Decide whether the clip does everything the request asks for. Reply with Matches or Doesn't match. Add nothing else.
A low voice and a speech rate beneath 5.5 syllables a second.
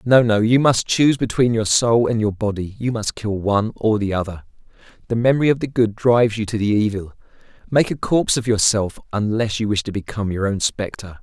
Doesn't match